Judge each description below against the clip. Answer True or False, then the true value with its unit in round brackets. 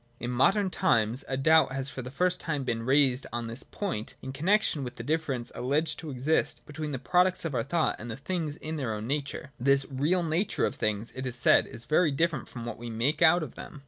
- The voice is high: False (140 Hz)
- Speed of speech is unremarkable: False (235 wpm)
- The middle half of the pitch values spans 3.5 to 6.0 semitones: True (4.4 semitones)